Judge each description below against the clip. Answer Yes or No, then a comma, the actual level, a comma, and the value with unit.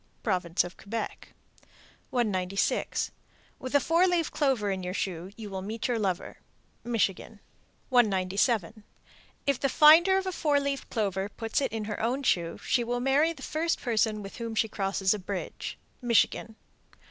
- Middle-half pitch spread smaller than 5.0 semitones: No, wide, 5.5 semitones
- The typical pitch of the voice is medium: No, high, 225 Hz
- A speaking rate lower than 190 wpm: Yes, average, 160 wpm